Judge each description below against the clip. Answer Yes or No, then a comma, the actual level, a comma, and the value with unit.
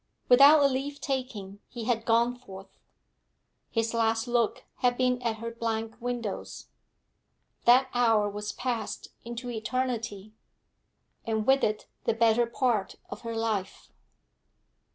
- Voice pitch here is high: Yes, high, 230 Hz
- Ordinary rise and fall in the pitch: No, narrow, 2.0 semitones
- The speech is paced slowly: Yes, slow, 130 wpm